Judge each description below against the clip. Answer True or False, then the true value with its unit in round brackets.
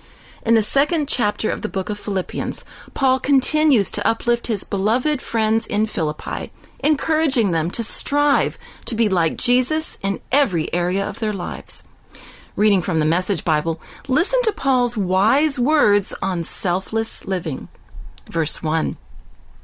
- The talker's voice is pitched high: True (220 Hz)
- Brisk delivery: False (145 wpm)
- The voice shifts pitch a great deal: True (6.0 semitones)